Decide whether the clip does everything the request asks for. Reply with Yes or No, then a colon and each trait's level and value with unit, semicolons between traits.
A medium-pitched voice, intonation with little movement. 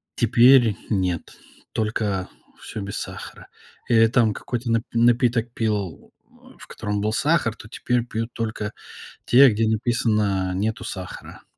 No: low, 110 Hz; narrow, 2.3 semitones